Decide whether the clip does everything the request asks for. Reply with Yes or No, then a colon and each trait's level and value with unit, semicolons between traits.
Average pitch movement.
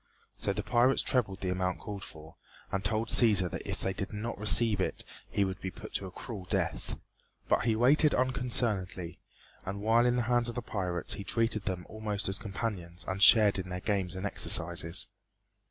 Yes: average, 3.7 semitones